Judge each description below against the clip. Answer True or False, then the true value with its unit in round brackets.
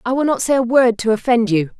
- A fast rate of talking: True (300 wpm)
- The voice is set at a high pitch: True (235 Hz)